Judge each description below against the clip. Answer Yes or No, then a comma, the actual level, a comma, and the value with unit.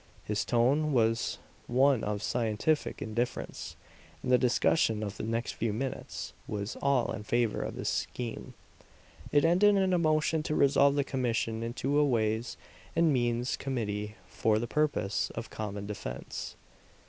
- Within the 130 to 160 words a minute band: Yes, average, 150 wpm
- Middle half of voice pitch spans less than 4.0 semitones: No, average, 4.4 semitones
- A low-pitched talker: Yes, low, 120 Hz